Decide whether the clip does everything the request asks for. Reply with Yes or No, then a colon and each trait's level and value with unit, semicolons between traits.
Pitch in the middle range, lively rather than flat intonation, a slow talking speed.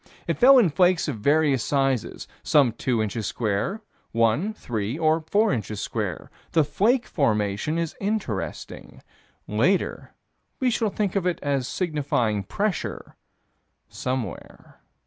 Yes: medium, 145 Hz; wide, 8.6 semitones; slow, 125 wpm